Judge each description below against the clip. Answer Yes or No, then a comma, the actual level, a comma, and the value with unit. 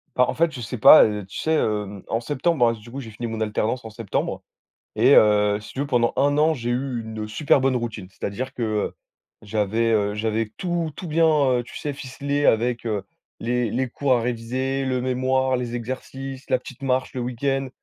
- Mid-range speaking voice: No, low, 125 Hz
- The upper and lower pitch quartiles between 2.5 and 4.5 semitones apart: Yes, average, 3.3 semitones